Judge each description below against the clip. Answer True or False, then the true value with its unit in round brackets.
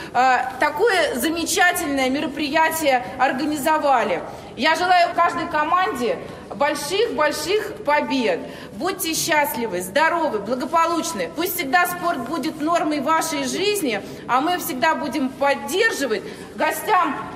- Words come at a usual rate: False (95 wpm)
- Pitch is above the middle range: True (315 Hz)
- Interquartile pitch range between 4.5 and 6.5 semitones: False (3.3 semitones)